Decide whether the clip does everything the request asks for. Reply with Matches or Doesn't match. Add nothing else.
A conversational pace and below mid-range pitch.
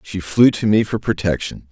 Doesn't match